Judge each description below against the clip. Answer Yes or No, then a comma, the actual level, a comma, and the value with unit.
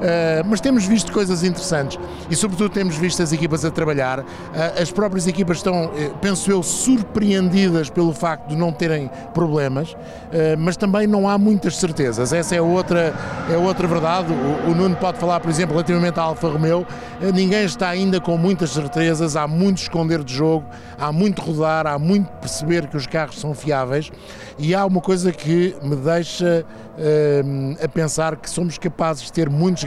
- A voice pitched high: No, medium, 170 Hz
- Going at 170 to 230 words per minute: Yes, fast, 185 wpm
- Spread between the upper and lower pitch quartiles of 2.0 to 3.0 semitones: Yes, average, 2.7 semitones